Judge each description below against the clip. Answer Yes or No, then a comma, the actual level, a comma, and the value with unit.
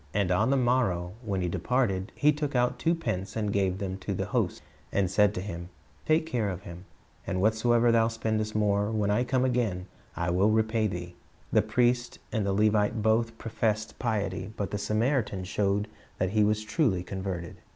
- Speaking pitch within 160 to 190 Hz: No, low, 105 Hz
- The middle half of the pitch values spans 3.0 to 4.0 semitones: Yes, average, 3.5 semitones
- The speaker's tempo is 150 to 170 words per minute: No, average, 190 wpm